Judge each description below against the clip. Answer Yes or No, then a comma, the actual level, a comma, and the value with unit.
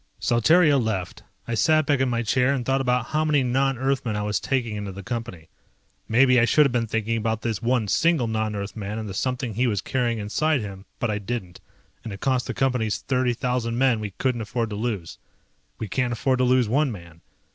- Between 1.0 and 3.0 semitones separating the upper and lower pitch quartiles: No, average, 3.4 semitones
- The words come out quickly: Yes, fast, 220 wpm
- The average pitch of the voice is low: Yes, low, 120 Hz